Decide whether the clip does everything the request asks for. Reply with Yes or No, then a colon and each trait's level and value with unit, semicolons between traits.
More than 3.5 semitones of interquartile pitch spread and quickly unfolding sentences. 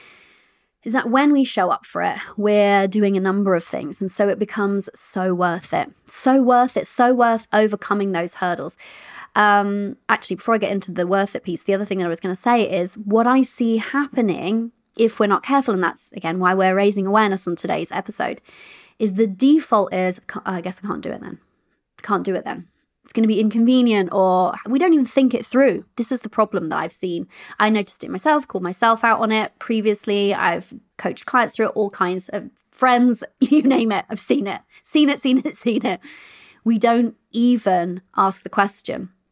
Yes: average, 3.9 semitones; fast, 210 wpm